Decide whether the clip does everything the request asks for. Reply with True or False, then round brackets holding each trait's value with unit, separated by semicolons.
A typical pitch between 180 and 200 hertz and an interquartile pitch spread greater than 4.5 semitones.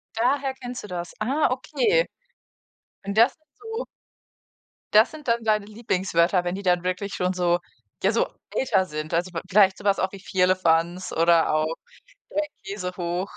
True (190 Hz; 4.9 semitones)